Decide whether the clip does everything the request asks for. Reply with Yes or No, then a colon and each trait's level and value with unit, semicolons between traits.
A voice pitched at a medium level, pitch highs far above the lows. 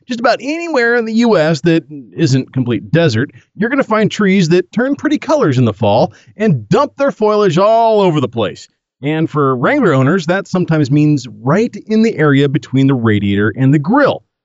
Yes: medium, 170 Hz; wide, 8.1 semitones